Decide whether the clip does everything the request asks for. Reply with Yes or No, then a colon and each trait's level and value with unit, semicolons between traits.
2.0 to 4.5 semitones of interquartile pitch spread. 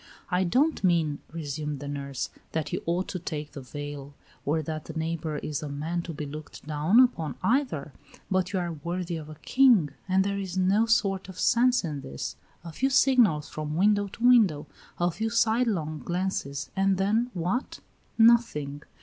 No: average, 5.2 semitones